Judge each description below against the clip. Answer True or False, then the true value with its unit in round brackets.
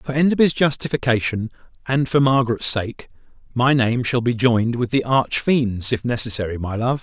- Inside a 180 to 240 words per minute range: False (170 wpm)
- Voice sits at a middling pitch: False (120 Hz)